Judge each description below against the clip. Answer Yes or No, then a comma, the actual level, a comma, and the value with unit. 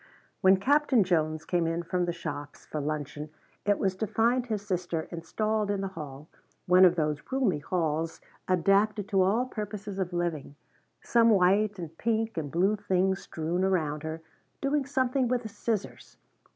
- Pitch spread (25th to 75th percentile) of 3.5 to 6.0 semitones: Yes, average, 4.7 semitones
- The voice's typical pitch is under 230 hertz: Yes, medium, 185 Hz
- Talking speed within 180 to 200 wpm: No, average, 165 wpm